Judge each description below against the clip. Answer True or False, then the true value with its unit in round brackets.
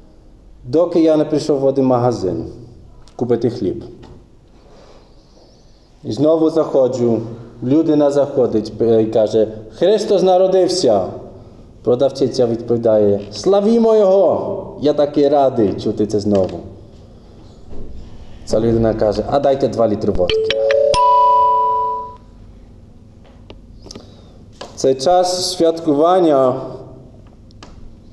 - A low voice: True (120 Hz)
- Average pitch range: False (6.1 semitones)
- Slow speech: True (85 wpm)